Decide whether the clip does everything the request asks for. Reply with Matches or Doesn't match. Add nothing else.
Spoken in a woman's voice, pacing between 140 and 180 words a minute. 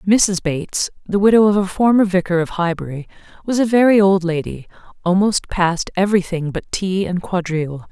Matches